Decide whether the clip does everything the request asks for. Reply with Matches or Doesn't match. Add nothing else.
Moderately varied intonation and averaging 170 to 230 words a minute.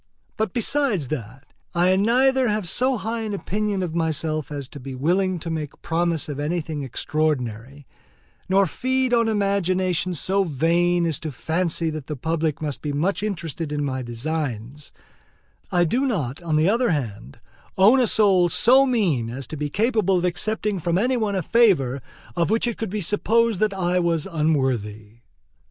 Doesn't match